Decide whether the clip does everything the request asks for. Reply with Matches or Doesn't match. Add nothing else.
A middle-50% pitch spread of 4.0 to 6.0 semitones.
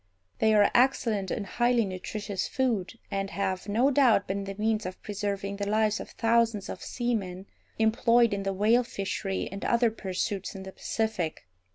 Doesn't match